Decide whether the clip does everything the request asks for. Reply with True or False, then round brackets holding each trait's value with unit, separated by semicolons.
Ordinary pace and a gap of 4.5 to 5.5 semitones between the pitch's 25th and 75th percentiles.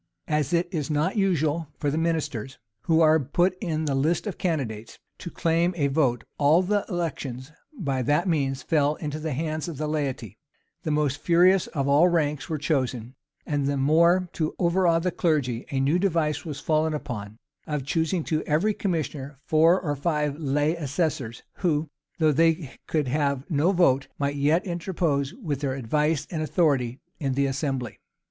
False (175 wpm; 3.1 semitones)